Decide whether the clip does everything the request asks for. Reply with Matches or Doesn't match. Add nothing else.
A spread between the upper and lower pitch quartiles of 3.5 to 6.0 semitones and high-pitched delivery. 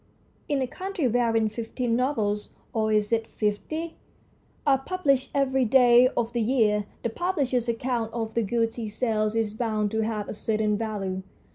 Doesn't match